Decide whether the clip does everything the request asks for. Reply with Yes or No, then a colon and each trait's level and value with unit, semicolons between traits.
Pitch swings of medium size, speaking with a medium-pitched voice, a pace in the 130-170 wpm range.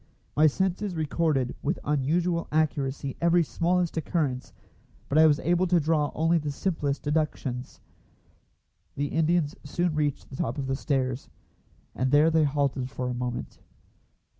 Yes: average, 3.4 semitones; medium, 150 Hz; average, 145 wpm